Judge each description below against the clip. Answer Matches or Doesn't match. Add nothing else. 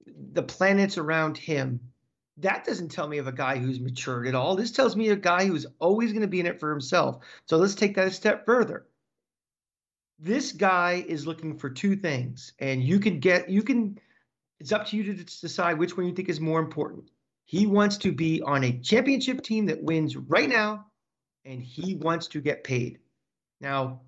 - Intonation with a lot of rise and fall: Matches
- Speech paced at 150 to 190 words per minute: Doesn't match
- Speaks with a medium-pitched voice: Matches